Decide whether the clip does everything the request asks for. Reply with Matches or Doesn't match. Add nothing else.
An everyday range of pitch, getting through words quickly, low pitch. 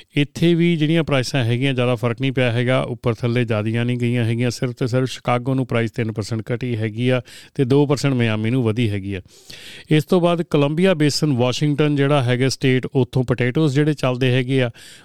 Matches